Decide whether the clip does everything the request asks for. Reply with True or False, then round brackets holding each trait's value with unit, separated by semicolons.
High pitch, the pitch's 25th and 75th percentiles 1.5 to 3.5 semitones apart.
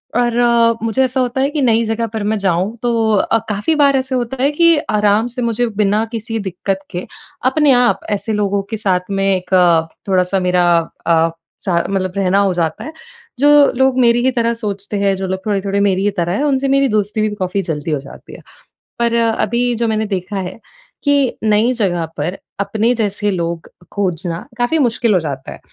False (210 Hz; 4.3 semitones)